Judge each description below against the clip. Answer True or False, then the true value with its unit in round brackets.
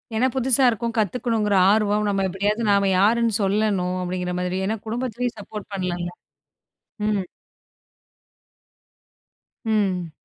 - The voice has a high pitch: True (210 Hz)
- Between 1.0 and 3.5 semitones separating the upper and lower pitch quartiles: True (3.2 semitones)